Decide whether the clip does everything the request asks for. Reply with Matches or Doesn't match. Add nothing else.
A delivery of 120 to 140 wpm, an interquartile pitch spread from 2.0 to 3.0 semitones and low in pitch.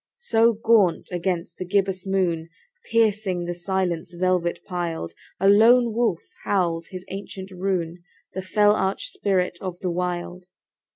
Doesn't match